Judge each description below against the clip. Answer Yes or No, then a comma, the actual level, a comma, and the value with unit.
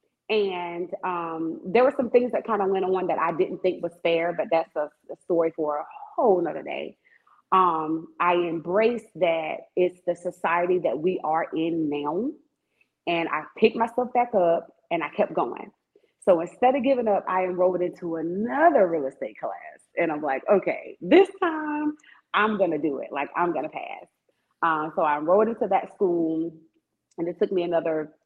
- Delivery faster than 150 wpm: Yes, average, 190 wpm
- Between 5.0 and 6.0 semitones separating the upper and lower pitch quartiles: Yes, average, 5.3 semitones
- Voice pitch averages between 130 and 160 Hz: No, medium, 180 Hz